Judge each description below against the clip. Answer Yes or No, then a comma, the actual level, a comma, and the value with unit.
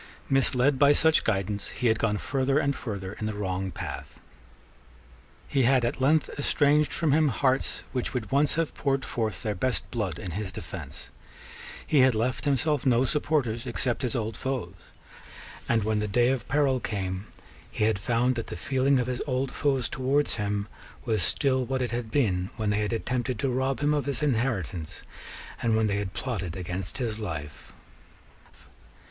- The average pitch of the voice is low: Yes, low, 120 Hz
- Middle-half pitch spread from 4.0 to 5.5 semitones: Yes, average, 4.4 semitones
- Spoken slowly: No, average, 180 wpm